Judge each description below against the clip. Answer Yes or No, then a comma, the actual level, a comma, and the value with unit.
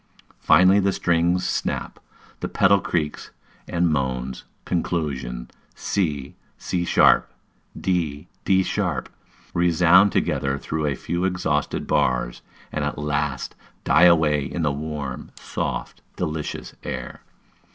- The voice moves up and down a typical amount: Yes, average, 3.9 semitones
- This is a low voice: Yes, very low, 80 Hz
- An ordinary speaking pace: No, slow, 115 wpm